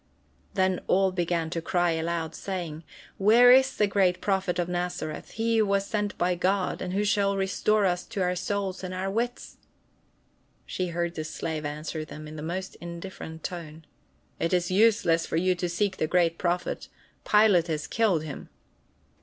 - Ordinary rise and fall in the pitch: Yes, average, 3.0 semitones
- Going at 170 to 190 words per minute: Yes, average, 175 wpm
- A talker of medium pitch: Yes, medium, 180 Hz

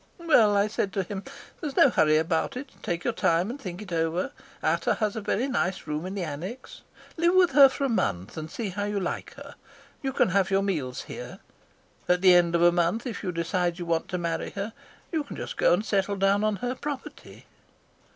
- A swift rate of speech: Yes, fast, 230 wpm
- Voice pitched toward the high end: Yes, high, 195 Hz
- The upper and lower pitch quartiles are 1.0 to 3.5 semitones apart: No, wide, 5.4 semitones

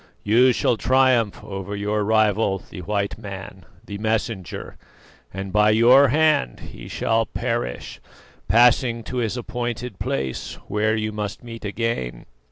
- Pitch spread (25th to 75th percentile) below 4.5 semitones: Yes, average, 2.8 semitones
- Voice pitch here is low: Yes, low, 110 Hz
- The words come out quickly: No, slow, 135 wpm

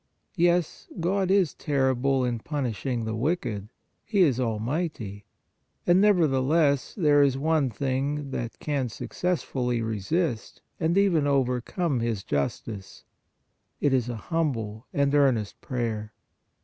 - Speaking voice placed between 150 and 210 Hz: No, low, 135 Hz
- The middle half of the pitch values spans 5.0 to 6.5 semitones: Yes, wide, 5.5 semitones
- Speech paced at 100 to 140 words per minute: Yes, slow, 135 wpm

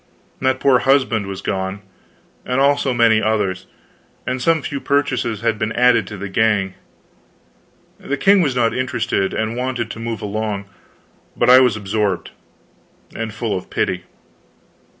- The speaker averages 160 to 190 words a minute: No, average, 150 wpm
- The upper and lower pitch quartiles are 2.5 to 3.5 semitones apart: No, average, 3.9 semitones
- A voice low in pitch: Yes, low, 115 Hz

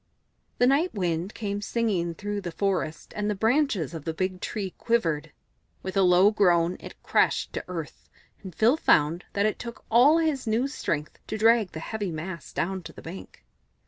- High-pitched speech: Yes, high, 195 Hz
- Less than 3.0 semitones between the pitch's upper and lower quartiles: No, average, 4.7 semitones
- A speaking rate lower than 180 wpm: No, average, 185 wpm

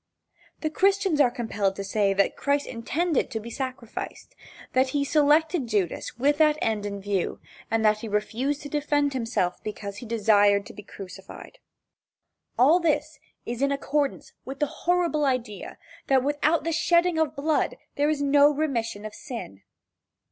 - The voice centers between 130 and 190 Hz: No, very high, 270 Hz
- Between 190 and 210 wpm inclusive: No, average, 160 wpm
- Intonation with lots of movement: Yes, wide, 5.8 semitones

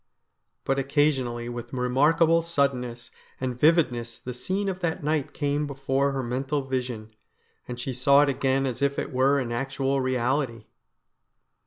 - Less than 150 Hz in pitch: Yes, low, 135 Hz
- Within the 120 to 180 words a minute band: Yes, average, 150 wpm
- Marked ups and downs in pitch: No, narrow, 2.5 semitones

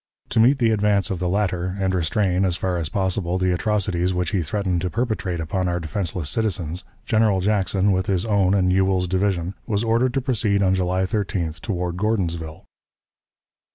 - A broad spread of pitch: No, narrow, 2.6 semitones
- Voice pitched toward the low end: Yes, very low, 95 Hz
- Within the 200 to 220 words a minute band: No, average, 180 wpm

